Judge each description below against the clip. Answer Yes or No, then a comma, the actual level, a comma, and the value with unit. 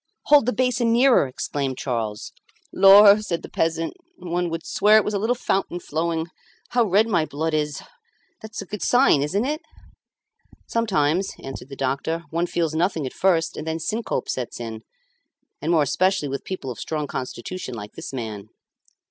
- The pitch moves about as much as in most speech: No, wide, 6.3 semitones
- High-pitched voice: No, medium, 165 Hz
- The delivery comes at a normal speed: Yes, average, 175 wpm